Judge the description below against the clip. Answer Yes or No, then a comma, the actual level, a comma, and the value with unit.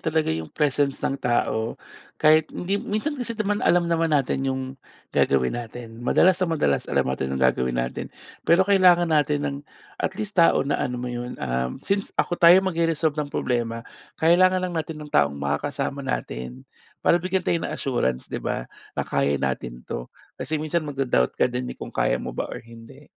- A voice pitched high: No, medium, 140 Hz